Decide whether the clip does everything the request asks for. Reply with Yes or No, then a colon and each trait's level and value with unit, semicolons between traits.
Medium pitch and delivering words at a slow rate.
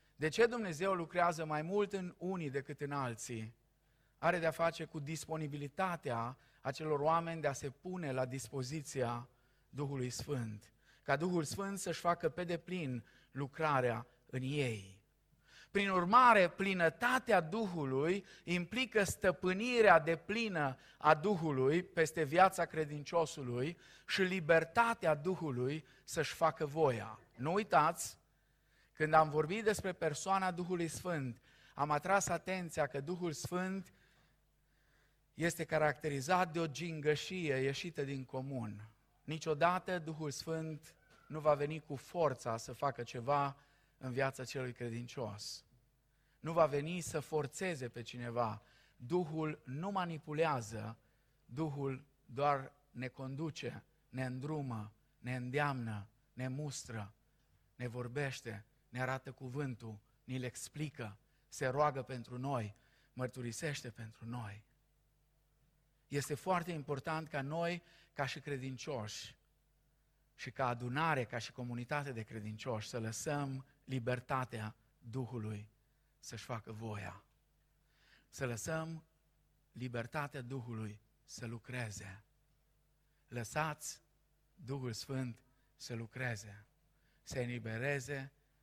Yes: medium, 145 Hz; slow, 110 wpm